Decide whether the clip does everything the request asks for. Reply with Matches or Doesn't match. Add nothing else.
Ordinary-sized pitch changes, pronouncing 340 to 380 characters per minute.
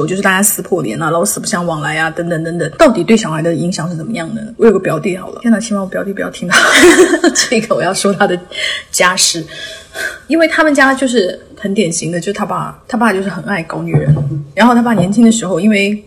Matches